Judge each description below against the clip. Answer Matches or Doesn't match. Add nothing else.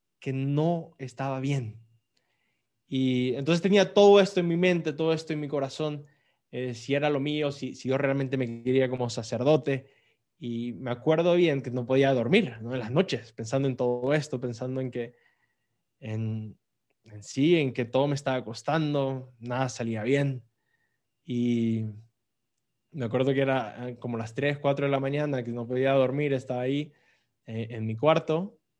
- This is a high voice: Doesn't match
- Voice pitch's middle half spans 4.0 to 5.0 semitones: Doesn't match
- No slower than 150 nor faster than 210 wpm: Matches